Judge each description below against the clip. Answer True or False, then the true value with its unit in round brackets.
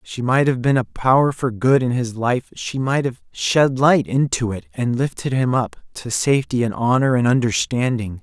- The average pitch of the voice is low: True (125 Hz)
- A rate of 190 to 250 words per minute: True (205 wpm)